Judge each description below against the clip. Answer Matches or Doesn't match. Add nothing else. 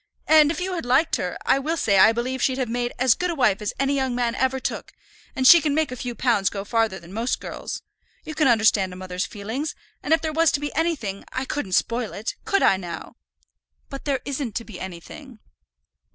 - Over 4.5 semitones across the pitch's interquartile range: Matches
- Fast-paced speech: Matches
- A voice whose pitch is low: Doesn't match